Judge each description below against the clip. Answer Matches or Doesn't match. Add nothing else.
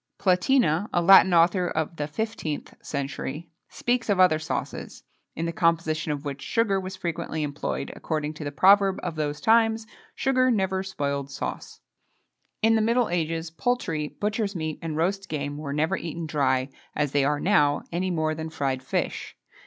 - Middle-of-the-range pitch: Matches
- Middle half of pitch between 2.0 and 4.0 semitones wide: Doesn't match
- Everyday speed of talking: Matches